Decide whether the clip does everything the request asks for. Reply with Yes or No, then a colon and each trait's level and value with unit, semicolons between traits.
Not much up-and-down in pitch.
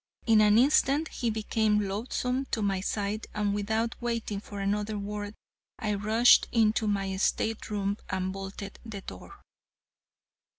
Yes: narrow, 1.9 semitones